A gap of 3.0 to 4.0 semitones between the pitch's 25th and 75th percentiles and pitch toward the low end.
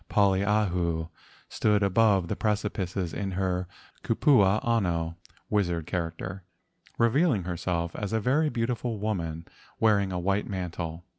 Yes: average, 3.5 semitones; very low, 95 Hz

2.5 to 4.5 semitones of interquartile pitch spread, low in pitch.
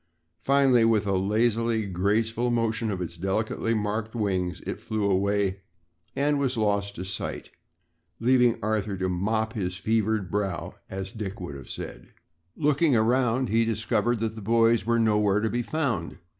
Yes: average, 2.8 semitones; low, 110 Hz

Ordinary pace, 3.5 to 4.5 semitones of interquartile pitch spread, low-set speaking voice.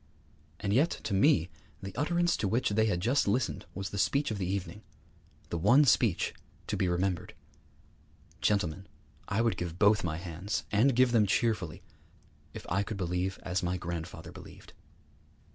Yes: average, 165 wpm; average, 4.1 semitones; low, 100 Hz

